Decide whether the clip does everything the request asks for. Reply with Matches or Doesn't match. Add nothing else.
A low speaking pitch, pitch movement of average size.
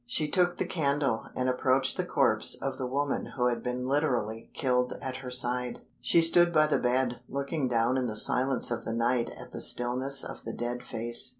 Doesn't match